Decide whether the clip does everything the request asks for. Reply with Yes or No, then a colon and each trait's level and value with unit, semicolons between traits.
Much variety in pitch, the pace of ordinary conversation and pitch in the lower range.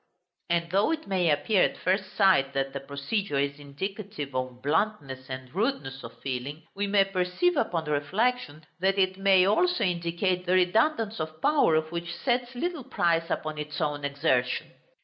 No: wide, 5.8 semitones; average, 165 wpm; medium, 175 Hz